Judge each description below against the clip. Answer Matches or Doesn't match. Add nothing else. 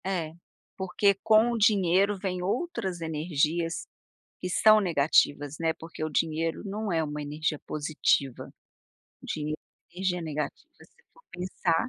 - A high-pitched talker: Doesn't match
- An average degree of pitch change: Matches